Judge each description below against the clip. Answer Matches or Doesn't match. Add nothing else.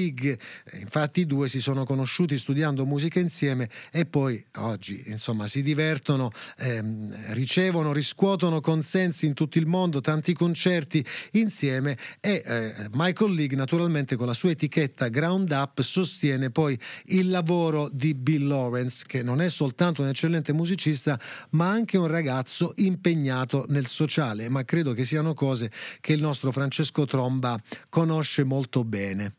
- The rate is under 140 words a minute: Doesn't match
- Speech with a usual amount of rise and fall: Matches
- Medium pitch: Matches